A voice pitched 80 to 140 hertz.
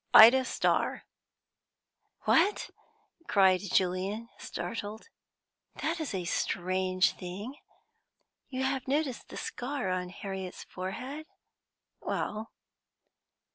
No: high, 210 Hz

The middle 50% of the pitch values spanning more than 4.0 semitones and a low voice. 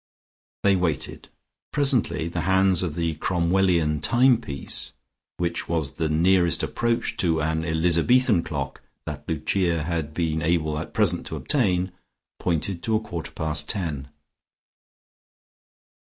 No: average, 3.0 semitones; very low, 85 Hz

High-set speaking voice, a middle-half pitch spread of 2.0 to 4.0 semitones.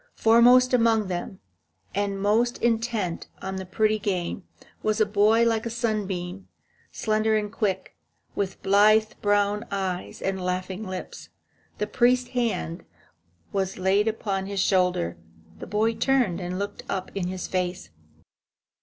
Yes: high, 205 Hz; average, 2.9 semitones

